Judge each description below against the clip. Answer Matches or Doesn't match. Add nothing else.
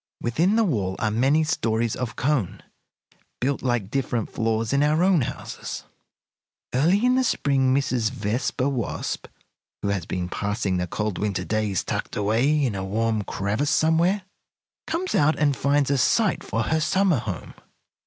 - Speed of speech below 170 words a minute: Matches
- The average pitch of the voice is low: Matches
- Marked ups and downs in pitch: Matches